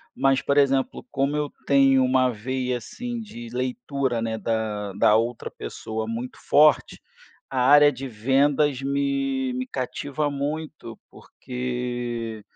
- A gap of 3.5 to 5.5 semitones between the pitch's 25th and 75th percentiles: No, average, 2.8 semitones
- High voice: No, low, 130 Hz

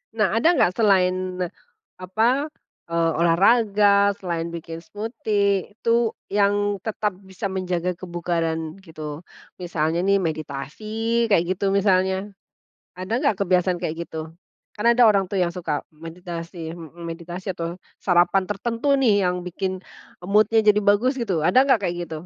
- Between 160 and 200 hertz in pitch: Yes, medium, 185 Hz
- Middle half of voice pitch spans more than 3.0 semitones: Yes, average, 3.4 semitones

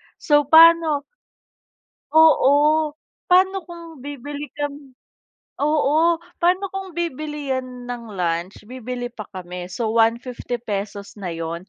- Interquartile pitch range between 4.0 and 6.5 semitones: Yes, average, 5.3 semitones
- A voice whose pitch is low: No, very high, 285 Hz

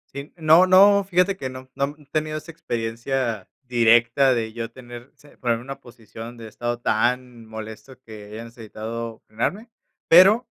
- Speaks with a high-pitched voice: No, low, 120 Hz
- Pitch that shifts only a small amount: No, average, 4.4 semitones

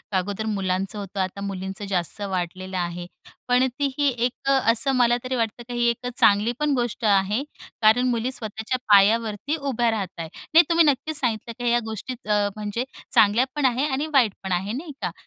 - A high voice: Yes, high, 220 Hz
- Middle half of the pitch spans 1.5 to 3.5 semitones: No, average, 4.1 semitones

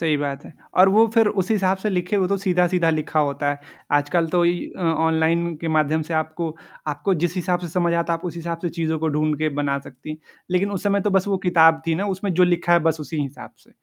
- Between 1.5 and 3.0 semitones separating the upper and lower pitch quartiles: Yes, narrow, 2.6 semitones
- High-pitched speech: No, medium, 170 Hz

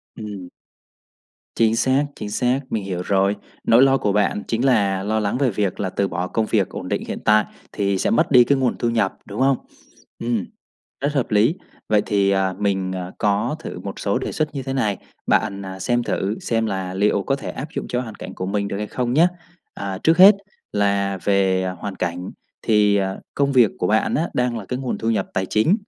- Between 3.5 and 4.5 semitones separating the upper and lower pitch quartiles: Yes, average, 4.0 semitones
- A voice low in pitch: Yes, low, 105 Hz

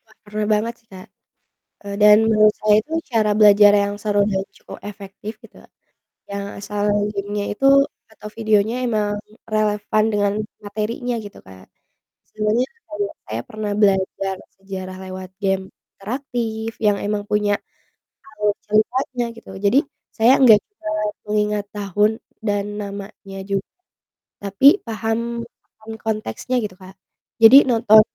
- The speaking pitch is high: Yes, high, 210 Hz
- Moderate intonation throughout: No, narrow, 1.6 semitones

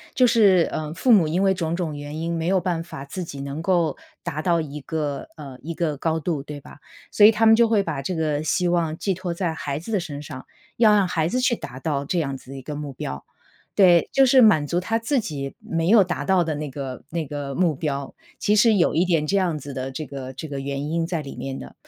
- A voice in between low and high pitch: Yes, medium, 160 Hz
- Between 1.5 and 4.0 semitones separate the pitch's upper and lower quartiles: No, average, 4.4 semitones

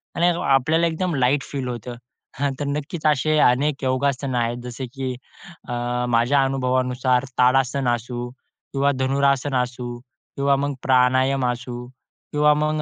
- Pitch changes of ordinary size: No, narrow, 2.2 semitones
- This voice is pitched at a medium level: No, low, 130 Hz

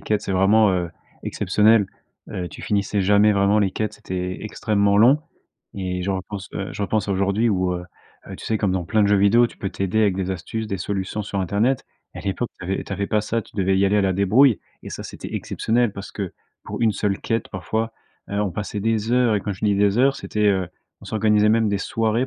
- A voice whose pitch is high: No, low, 100 Hz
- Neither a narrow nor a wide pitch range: No, narrow, 2.1 semitones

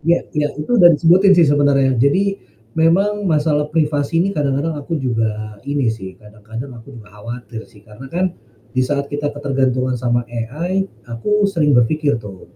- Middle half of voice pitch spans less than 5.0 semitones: No, wide, 5.6 semitones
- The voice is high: No, medium, 140 Hz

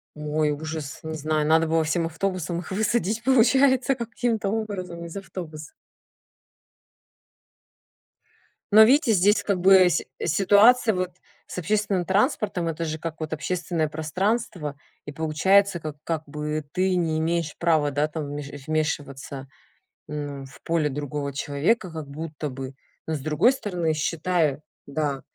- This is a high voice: No, medium, 165 Hz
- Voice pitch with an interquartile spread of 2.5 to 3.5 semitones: No, average, 4.3 semitones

